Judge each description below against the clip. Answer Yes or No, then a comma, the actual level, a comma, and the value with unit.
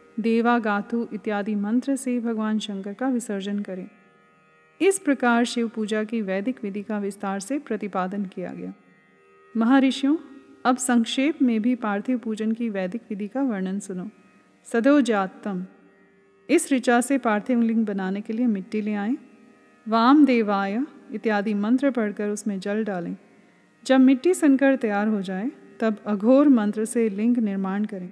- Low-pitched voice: No, high, 220 Hz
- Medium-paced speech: Yes, average, 145 wpm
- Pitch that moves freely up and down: No, average, 3.6 semitones